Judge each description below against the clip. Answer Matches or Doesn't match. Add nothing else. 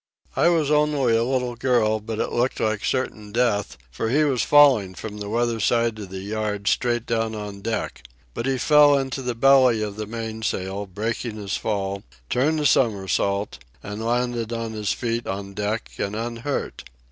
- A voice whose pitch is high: Doesn't match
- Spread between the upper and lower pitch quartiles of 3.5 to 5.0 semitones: Doesn't match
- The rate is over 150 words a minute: Matches